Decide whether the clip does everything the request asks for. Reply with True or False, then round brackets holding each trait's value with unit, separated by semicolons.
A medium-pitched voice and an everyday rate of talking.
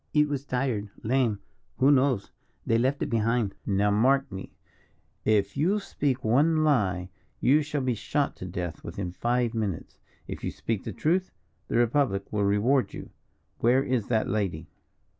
False (120 Hz; 160 wpm)